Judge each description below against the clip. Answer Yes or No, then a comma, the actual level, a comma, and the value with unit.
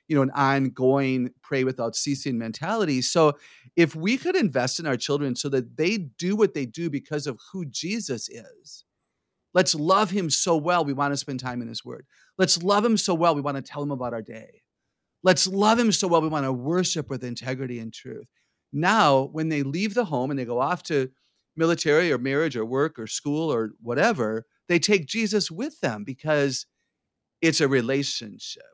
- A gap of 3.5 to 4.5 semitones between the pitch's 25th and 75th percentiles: No, average, 5.2 semitones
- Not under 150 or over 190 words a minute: No, average, 200 wpm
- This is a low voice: No, medium, 145 Hz